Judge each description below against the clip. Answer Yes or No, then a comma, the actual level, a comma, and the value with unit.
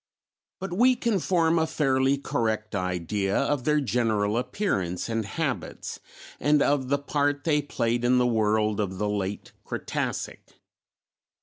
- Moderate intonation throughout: No, wide, 5.8 semitones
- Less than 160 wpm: Yes, average, 140 wpm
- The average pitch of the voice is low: Yes, low, 125 Hz